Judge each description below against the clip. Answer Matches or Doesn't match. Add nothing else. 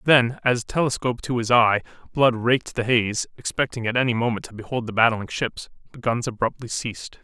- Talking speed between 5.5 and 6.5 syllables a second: Matches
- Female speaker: Doesn't match